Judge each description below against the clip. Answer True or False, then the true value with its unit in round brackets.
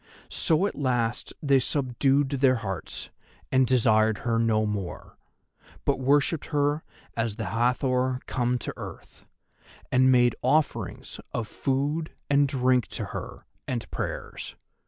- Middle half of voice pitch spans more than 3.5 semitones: False (3.2 semitones)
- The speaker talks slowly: True (130 wpm)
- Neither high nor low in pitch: False (130 Hz)